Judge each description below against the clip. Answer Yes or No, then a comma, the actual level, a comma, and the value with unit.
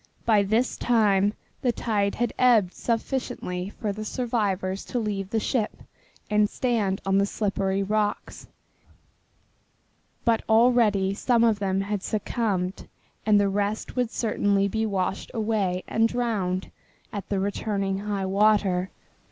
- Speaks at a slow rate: Yes, slow, 130 wpm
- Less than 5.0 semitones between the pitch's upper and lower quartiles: Yes, narrow, 2.4 semitones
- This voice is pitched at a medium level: No, high, 205 Hz